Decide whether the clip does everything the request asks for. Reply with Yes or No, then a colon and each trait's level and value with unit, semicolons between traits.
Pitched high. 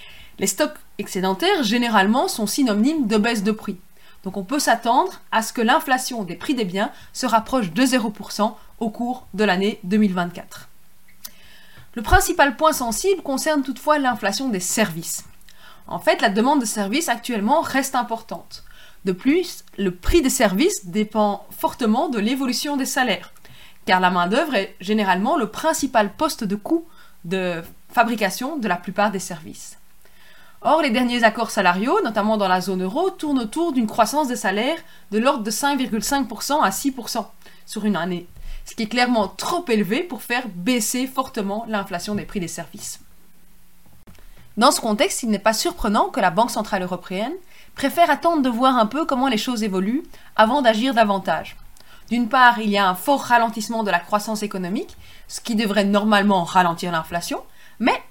Yes: high, 225 Hz